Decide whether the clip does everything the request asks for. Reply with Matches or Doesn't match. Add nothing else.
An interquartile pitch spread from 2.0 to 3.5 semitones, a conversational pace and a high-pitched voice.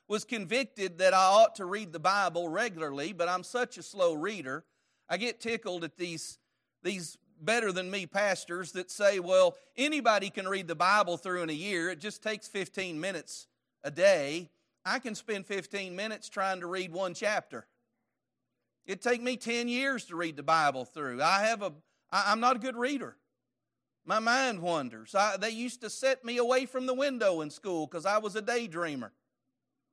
Doesn't match